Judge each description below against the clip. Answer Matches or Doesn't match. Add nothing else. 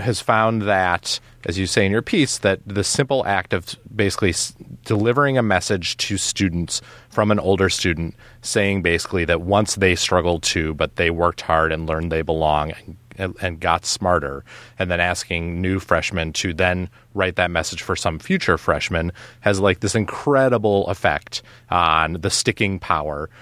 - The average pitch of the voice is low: Matches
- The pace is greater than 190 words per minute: Doesn't match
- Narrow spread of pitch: Doesn't match